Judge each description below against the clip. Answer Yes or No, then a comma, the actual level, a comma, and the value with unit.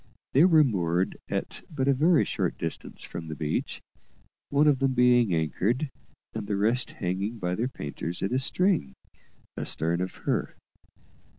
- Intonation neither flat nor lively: No, wide, 7.3 semitones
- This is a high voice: No, low, 115 Hz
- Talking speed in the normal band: Yes, average, 160 wpm